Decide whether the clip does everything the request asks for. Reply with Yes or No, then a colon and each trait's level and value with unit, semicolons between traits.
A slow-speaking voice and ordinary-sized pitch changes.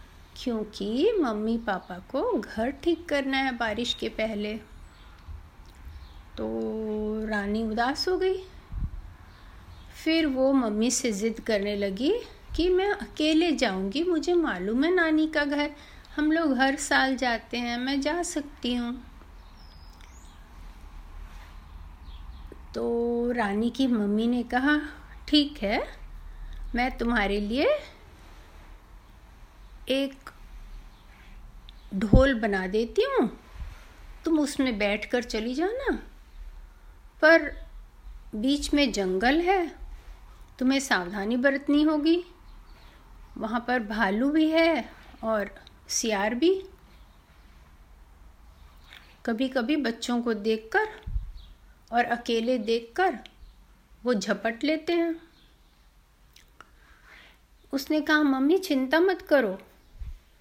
No: slow, 100 wpm; wide, 6.6 semitones